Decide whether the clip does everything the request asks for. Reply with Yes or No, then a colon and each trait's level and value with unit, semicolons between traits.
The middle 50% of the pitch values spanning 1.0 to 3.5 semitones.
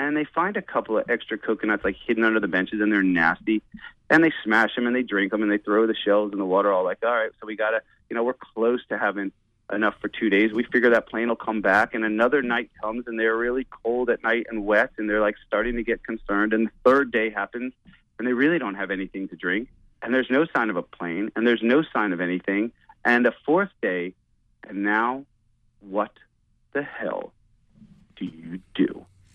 Yes: average, 2.8 semitones